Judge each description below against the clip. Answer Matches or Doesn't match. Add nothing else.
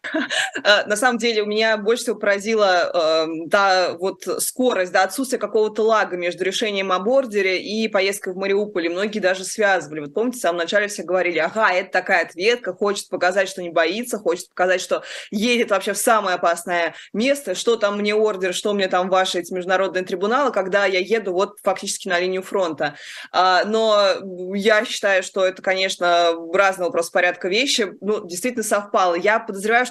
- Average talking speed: Doesn't match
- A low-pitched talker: Doesn't match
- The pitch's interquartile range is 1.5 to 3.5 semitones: Matches